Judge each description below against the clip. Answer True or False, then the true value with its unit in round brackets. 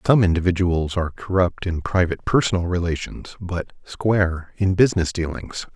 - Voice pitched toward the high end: False (90 Hz)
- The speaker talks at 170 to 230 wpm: False (135 wpm)